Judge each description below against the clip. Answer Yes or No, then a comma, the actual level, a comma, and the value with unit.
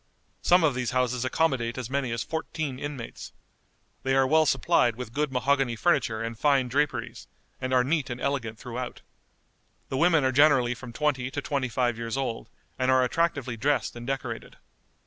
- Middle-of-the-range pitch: No, low, 130 Hz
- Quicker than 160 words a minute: Yes, average, 175 wpm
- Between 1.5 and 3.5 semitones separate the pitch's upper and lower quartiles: Yes, average, 2.9 semitones